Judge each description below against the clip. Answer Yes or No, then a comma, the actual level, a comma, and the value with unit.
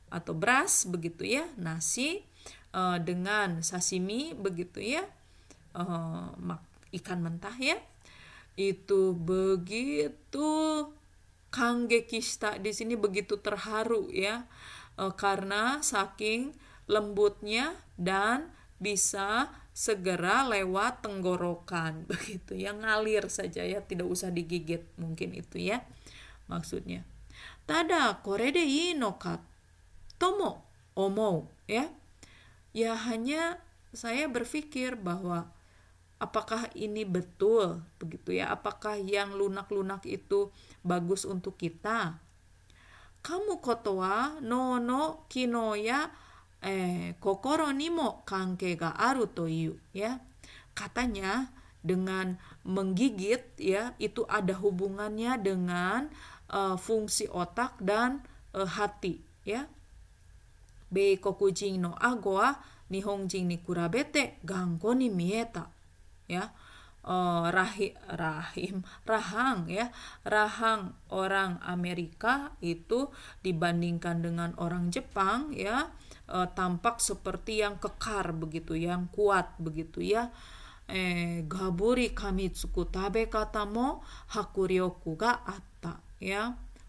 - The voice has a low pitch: No, high, 195 Hz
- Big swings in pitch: No, average, 4.5 semitones